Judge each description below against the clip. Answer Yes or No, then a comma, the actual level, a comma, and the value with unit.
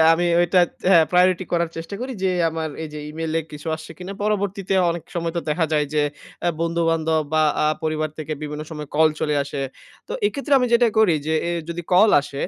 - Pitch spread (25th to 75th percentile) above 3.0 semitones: No, narrow, 2.6 semitones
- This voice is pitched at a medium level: Yes, medium, 165 Hz